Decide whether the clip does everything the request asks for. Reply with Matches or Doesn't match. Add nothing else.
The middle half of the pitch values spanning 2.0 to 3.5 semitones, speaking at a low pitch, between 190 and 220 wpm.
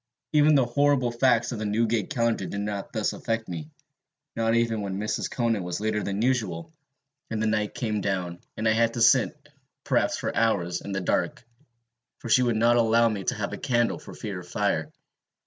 Matches